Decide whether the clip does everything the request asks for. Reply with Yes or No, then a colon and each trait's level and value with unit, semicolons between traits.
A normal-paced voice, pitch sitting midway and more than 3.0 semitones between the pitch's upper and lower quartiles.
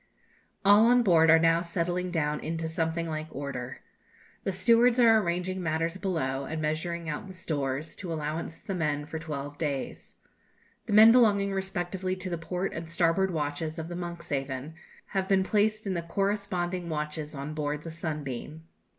Yes: average, 170 wpm; medium, 165 Hz; average, 3.6 semitones